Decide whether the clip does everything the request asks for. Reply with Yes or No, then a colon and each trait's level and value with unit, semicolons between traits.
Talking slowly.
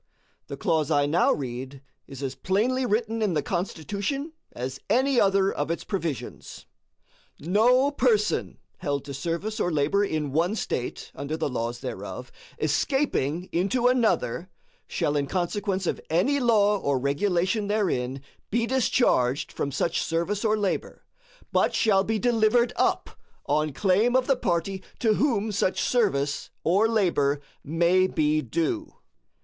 No: average, 145 wpm